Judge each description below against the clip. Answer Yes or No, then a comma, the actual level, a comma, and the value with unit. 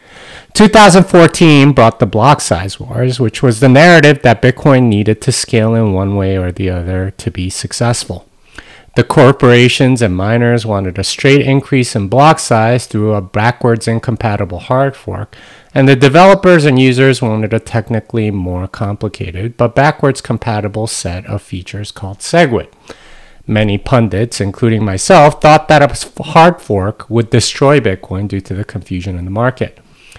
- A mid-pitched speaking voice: No, low, 115 Hz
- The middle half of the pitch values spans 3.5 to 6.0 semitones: Yes, average, 5.0 semitones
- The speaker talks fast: No, average, 155 wpm